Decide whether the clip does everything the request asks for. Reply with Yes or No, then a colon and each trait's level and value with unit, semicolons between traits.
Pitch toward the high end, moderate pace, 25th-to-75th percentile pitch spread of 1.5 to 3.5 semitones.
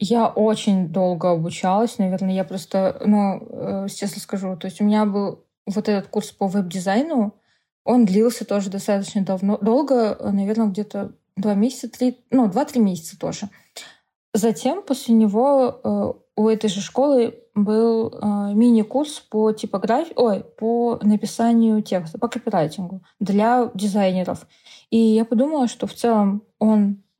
Yes: high, 215 Hz; average, 135 wpm; average, 2.8 semitones